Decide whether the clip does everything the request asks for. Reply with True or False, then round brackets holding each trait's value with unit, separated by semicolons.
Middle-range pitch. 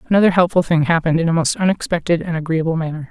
True (170 Hz)